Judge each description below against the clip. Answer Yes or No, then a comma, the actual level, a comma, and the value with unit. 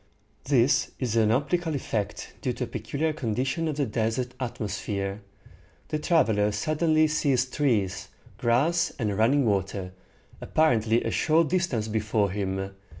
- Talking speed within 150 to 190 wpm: No, slow, 135 wpm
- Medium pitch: No, low, 120 Hz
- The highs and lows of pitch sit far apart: Yes, wide, 6.2 semitones